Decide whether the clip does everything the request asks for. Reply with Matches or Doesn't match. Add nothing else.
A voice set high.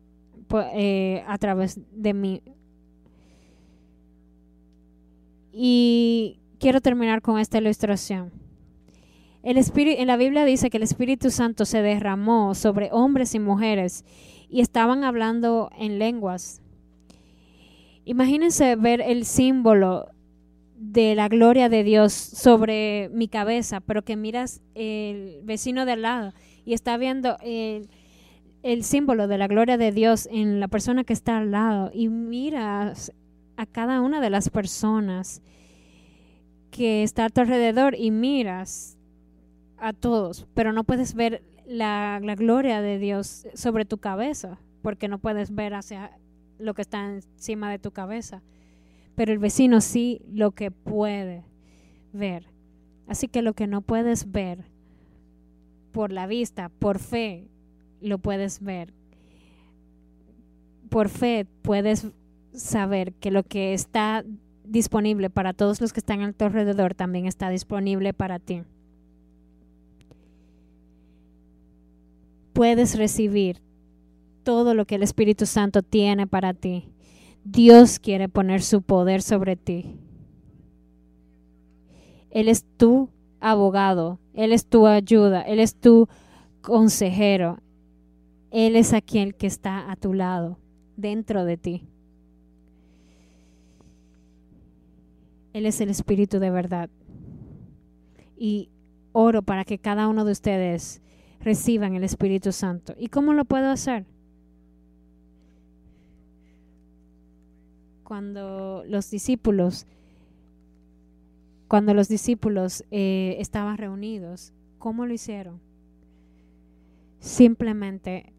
Matches